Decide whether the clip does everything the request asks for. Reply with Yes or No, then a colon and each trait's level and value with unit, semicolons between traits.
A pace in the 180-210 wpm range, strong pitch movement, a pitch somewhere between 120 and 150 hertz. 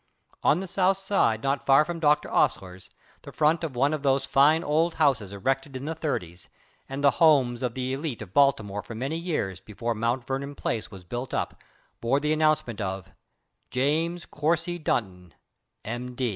No: average, 190 wpm; average, 5.0 semitones; low, 135 Hz